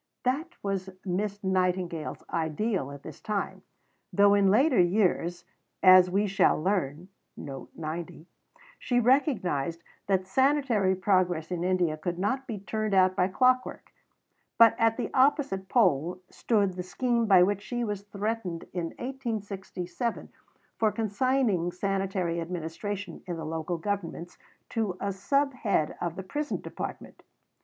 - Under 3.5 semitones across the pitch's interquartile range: No, average, 4.1 semitones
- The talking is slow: Yes, slow, 130 wpm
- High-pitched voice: Yes, high, 195 Hz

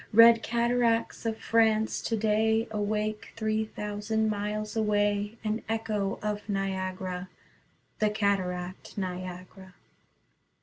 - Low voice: No, high, 210 Hz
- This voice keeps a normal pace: No, slow, 95 wpm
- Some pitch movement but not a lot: No, narrow, 1.9 semitones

